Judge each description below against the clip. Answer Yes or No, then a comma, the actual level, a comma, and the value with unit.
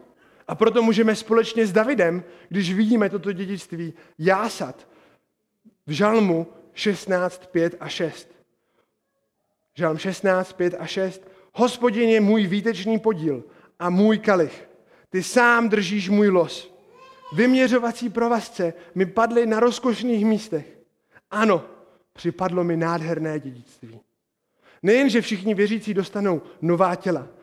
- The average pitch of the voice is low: No, high, 190 Hz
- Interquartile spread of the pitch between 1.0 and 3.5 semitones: No, average, 4.5 semitones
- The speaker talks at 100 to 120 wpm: Yes, slow, 115 wpm